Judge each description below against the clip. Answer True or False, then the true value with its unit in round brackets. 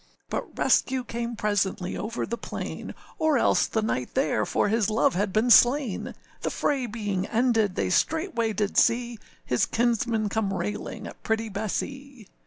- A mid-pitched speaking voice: False (225 Hz)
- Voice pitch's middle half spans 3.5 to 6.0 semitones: False (2.8 semitones)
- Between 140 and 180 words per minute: True (160 wpm)